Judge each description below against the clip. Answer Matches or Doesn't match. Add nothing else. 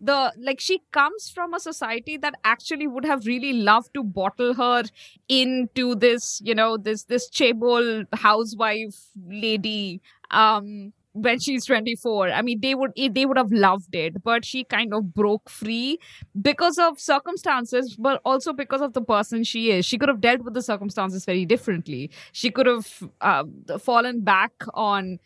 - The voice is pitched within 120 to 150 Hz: Doesn't match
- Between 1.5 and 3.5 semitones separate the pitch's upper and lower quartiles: Doesn't match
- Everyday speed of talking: Matches